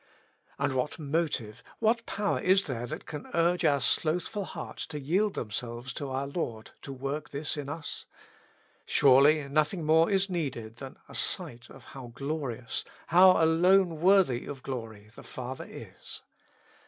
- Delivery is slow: No, average, 155 wpm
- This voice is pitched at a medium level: Yes, medium, 145 Hz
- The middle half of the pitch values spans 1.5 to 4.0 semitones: No, average, 4.8 semitones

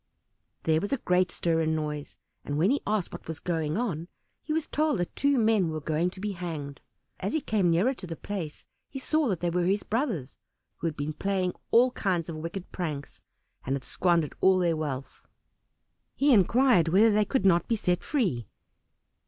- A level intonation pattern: No, average, 5.2 semitones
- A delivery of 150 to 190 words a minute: No, average, 200 wpm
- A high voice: No, medium, 180 Hz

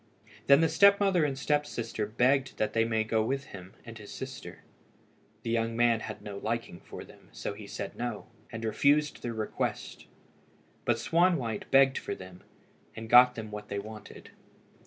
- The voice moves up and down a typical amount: Yes, average, 4.1 semitones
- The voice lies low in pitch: Yes, low, 115 Hz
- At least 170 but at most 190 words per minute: Yes, average, 180 wpm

